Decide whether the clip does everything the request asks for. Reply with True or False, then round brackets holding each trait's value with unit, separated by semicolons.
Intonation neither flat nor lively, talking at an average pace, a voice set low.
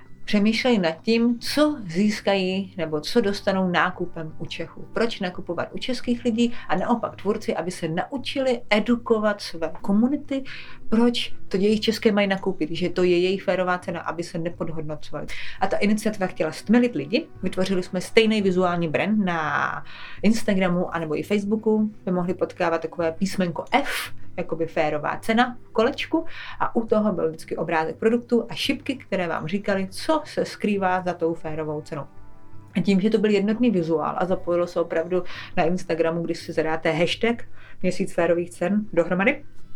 False (4.6 semitones; 160 wpm; 185 Hz)